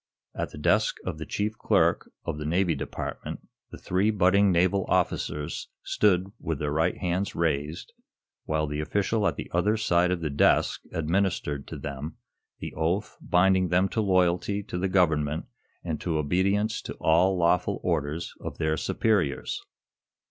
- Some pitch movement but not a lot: Yes, average, 3.6 semitones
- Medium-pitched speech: No, very low, 90 Hz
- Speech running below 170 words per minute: Yes, average, 160 wpm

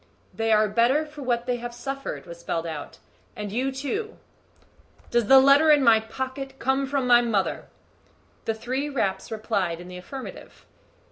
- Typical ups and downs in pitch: Yes, average, 4.1 semitones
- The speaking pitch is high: Yes, high, 240 Hz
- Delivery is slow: No, average, 165 wpm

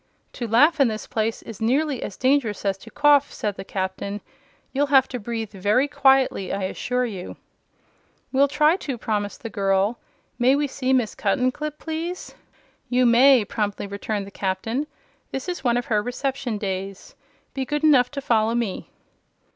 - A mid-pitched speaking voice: No, high, 240 Hz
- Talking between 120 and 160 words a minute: No, average, 170 wpm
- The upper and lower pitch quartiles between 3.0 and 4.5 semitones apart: No, average, 4.9 semitones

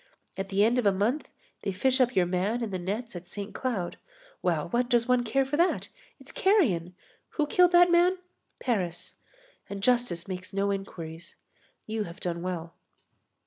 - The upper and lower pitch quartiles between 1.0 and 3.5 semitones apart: No, wide, 5.6 semitones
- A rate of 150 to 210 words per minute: Yes, average, 180 wpm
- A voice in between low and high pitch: No, high, 205 Hz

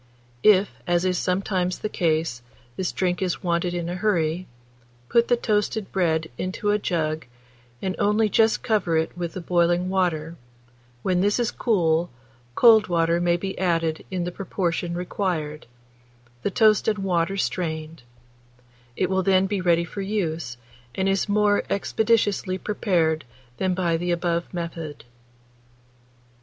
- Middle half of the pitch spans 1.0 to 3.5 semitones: Yes, average, 2.8 semitones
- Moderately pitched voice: Yes, medium, 180 Hz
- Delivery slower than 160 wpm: Yes, average, 145 wpm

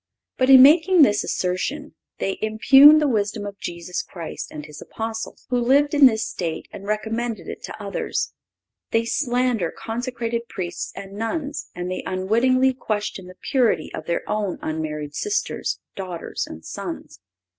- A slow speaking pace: No, average, 155 wpm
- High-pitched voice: Yes, high, 220 Hz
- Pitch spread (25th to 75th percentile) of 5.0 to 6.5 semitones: Yes, wide, 5.6 semitones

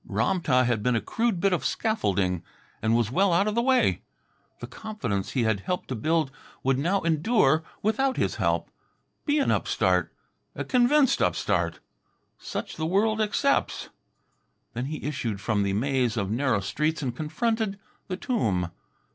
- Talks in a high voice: No, medium, 155 Hz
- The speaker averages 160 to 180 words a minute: Yes, average, 165 wpm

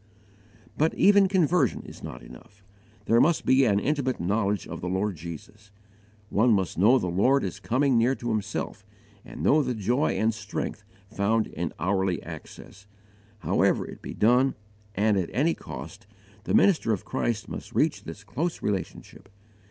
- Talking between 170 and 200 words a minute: No, average, 160 wpm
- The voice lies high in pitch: No, low, 110 Hz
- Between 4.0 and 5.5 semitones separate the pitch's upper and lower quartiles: Yes, average, 5.2 semitones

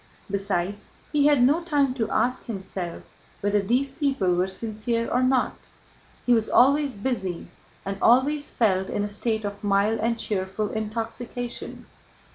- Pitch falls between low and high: No, high, 225 Hz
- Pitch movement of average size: Yes, average, 4.2 semitones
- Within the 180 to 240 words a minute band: No, average, 145 wpm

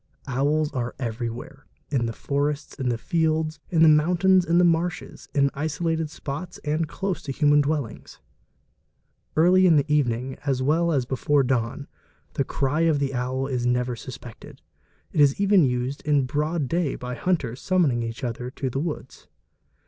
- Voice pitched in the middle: Yes, medium, 145 Hz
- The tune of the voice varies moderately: Yes, average, 4.0 semitones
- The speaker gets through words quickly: No, average, 165 wpm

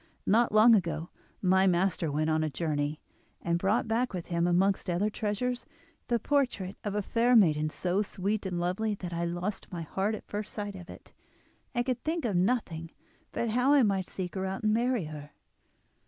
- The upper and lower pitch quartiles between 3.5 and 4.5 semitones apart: Yes, average, 4.2 semitones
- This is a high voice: Yes, high, 195 Hz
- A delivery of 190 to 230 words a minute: Yes, average, 195 wpm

